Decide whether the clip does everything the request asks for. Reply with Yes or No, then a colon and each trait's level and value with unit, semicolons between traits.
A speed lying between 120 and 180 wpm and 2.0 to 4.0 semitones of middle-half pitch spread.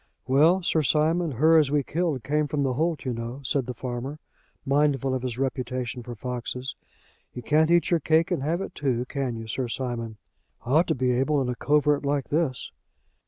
No: average, 200 wpm; average, 3.3 semitones